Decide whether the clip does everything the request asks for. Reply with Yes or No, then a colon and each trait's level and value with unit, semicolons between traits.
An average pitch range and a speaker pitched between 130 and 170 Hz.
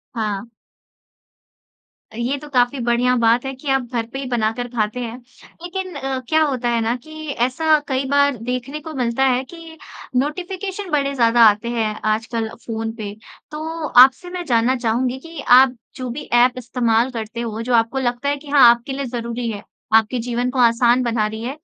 No: average, 3.0 semitones; very high, 250 Hz